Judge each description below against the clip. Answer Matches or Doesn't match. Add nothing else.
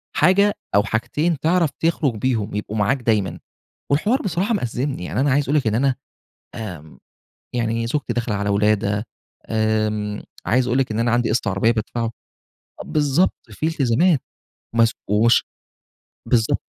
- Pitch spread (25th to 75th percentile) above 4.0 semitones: Matches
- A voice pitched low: Matches